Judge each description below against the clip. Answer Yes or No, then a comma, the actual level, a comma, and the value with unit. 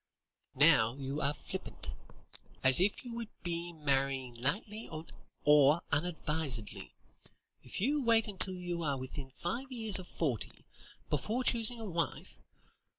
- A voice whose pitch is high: No, medium, 165 Hz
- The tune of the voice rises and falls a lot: Yes, wide, 7.4 semitones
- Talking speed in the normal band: No, slow, 130 wpm